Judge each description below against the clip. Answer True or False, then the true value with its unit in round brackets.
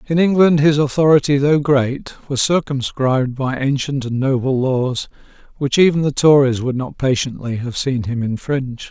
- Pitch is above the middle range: False (135 Hz)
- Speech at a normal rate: True (160 wpm)